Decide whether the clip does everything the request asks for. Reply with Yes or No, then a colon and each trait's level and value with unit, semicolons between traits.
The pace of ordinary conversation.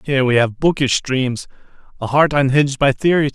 Yes: average, 180 wpm